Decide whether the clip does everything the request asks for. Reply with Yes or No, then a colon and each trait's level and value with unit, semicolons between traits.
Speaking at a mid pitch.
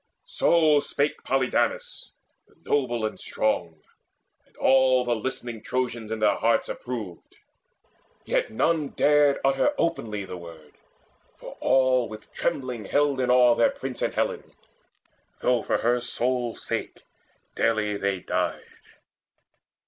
No: low, 125 Hz